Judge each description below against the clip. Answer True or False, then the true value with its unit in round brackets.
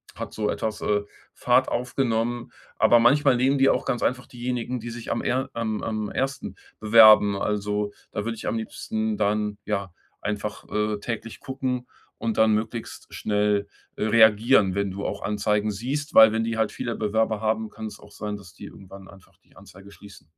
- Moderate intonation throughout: False (2.3 semitones)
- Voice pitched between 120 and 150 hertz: False (110 Hz)